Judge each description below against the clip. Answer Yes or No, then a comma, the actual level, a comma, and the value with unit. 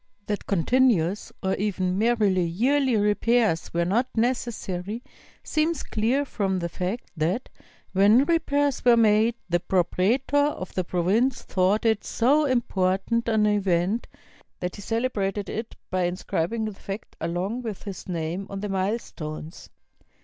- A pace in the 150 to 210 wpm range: No, average, 140 wpm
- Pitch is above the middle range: Yes, high, 205 Hz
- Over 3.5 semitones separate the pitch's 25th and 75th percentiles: Yes, average, 4.4 semitones